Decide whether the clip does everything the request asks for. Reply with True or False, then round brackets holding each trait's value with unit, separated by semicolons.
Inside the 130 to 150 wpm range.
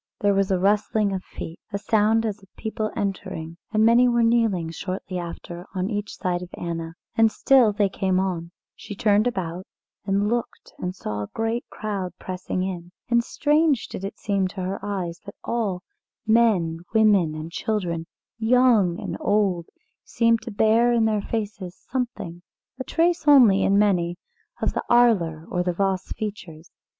False (170 wpm)